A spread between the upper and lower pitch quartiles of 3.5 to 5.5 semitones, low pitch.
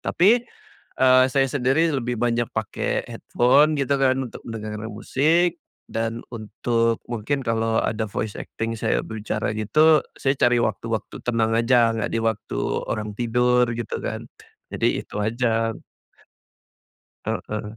No: average, 2.9 semitones; low, 115 Hz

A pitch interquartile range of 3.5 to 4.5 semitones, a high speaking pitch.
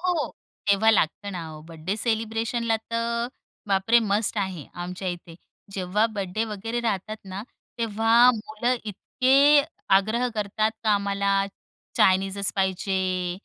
No: average, 3.1 semitones; high, 210 Hz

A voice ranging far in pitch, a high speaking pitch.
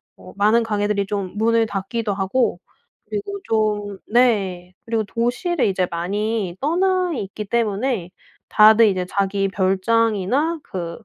No: average, 3.2 semitones; high, 210 Hz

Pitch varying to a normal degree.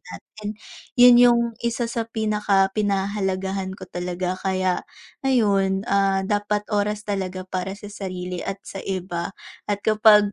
No: narrow, 1.9 semitones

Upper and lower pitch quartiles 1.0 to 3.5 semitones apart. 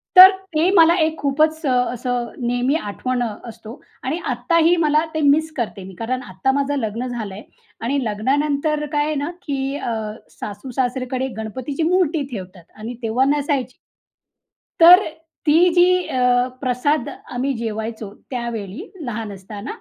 No: average, 4.6 semitones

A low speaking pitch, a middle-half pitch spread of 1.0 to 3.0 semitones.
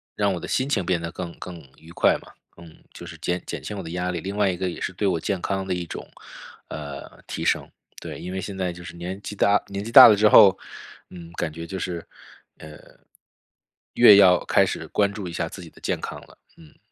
Yes: very low, 90 Hz; narrow, 2.6 semitones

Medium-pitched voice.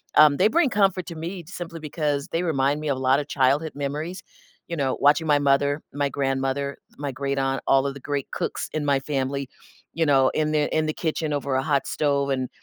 Yes: medium, 145 Hz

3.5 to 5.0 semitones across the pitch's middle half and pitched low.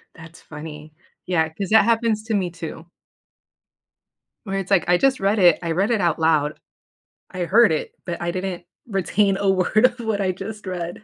No: average, 3.8 semitones; medium, 185 Hz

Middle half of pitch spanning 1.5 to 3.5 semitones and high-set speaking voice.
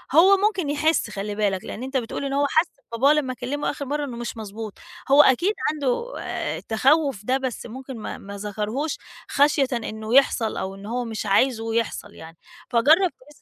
No: average, 5.0 semitones; very high, 255 Hz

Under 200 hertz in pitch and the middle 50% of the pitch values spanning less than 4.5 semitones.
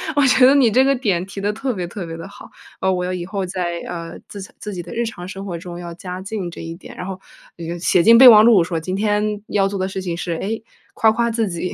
Yes: high, 190 Hz; average, 3.7 semitones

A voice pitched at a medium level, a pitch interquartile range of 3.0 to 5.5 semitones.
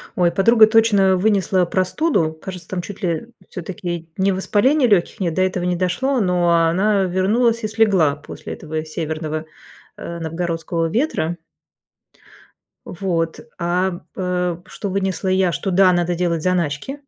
No: medium, 180 Hz; narrow, 2.6 semitones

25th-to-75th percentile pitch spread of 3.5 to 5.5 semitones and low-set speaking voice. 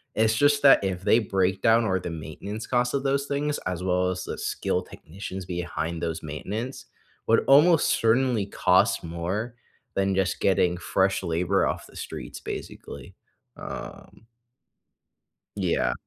Yes: average, 4.7 semitones; very low, 95 Hz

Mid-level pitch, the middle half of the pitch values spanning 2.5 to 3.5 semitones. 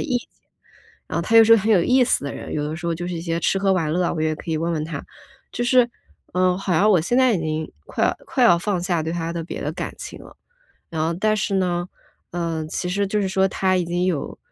Yes: medium, 175 Hz; average, 3.0 semitones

